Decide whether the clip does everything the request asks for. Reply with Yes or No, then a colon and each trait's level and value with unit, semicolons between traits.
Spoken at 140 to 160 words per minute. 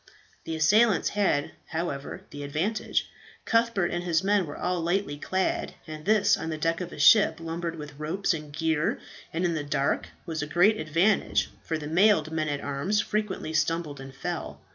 No: average, 185 wpm